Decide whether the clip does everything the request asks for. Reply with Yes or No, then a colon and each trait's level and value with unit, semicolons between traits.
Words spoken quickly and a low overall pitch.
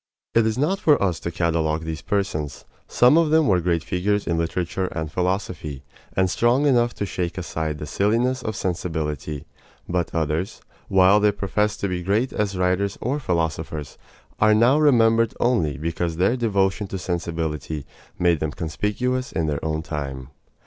No: average, 165 wpm; very low, 90 Hz